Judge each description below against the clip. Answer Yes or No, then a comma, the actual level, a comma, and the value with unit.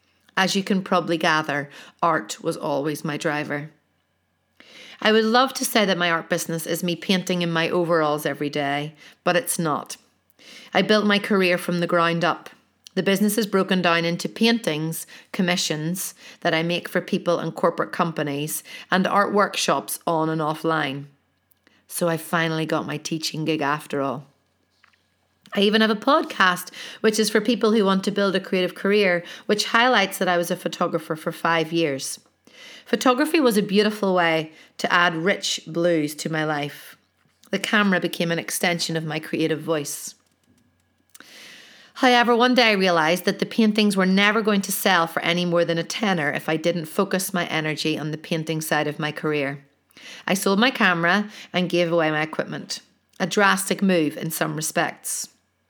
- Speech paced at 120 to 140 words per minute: No, average, 175 wpm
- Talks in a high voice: No, medium, 175 Hz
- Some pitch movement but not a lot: Yes, average, 4.0 semitones